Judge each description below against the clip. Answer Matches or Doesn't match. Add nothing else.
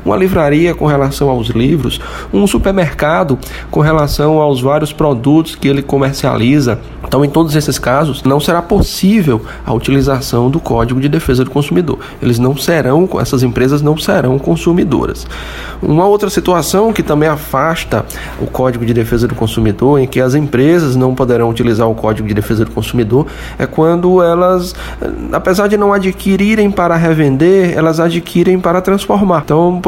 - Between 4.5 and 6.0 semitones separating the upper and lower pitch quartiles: Matches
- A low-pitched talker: Doesn't match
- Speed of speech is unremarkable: Matches